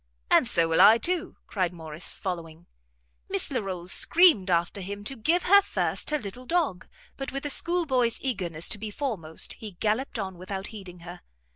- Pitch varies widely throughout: Yes, wide, 7.2 semitones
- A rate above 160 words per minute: Yes, average, 175 wpm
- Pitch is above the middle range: Yes, high, 205 Hz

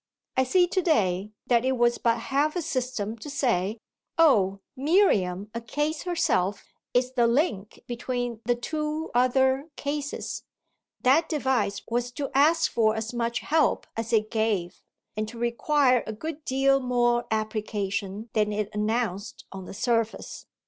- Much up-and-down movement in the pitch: No, average, 4.4 semitones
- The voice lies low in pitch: No, high, 240 Hz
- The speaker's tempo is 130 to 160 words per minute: Yes, average, 150 wpm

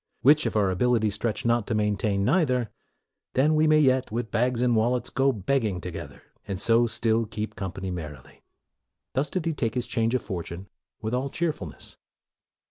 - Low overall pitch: Yes, low, 115 Hz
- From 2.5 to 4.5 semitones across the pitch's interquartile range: Yes, average, 4.0 semitones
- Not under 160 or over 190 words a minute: Yes, average, 185 wpm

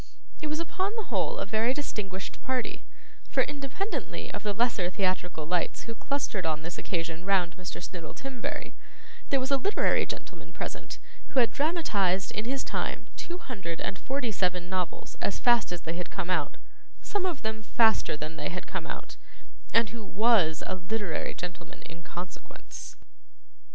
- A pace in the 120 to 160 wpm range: No, average, 170 wpm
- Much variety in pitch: Yes, wide, 6.5 semitones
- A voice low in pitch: No, high, 200 Hz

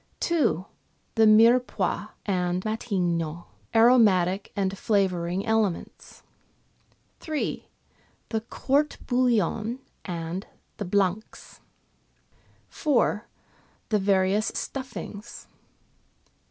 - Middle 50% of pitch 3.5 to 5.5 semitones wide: Yes, average, 4.1 semitones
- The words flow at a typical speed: No, slow, 100 wpm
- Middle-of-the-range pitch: No, high, 205 Hz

